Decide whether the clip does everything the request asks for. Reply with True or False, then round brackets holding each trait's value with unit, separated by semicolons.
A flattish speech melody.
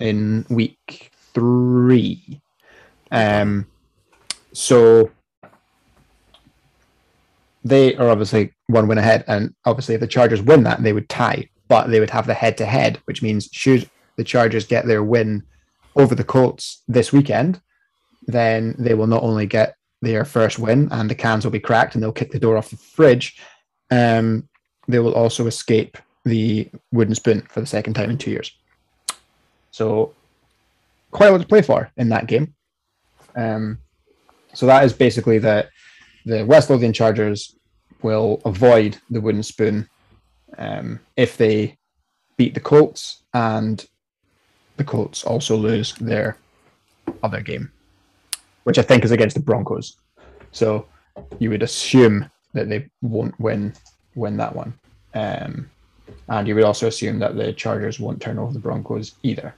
True (2.2 semitones)